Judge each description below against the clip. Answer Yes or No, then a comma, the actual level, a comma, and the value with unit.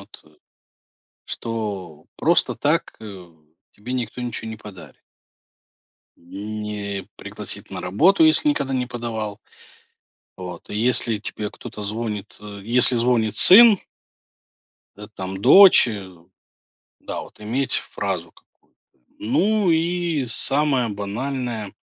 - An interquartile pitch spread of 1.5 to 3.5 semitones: No, average, 4.0 semitones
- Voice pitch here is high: No, low, 110 Hz